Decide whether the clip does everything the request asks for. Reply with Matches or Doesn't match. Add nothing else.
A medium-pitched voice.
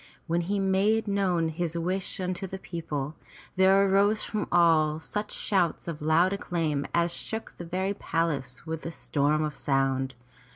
Matches